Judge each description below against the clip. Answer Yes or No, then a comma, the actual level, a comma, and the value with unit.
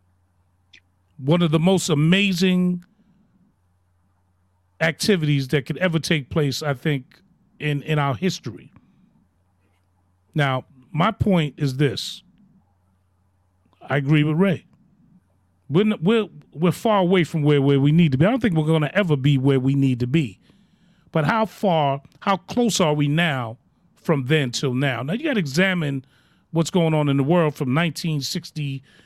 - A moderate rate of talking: Yes, average, 160 wpm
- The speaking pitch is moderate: Yes, medium, 150 Hz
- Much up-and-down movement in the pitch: Yes, wide, 5.8 semitones